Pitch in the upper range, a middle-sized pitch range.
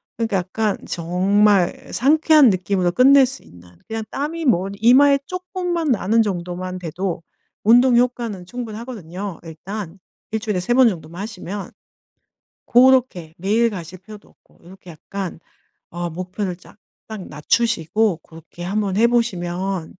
Yes: high, 200 Hz; average, 4.9 semitones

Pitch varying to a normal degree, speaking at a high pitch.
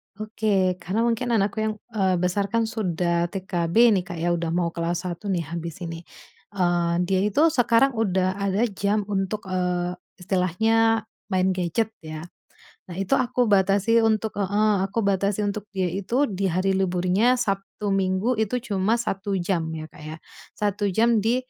Yes: average, 3.3 semitones; high, 195 Hz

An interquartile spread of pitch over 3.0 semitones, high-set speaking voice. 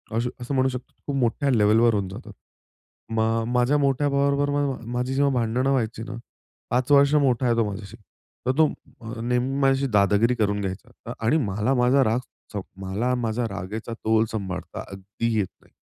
No: average, 3.4 semitones; low, 120 Hz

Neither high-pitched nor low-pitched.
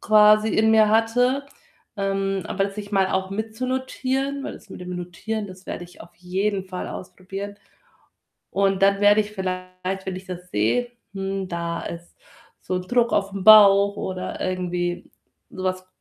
No: high, 195 Hz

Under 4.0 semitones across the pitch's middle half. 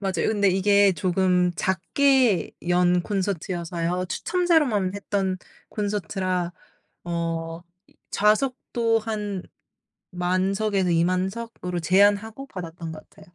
Yes: average, 2.9 semitones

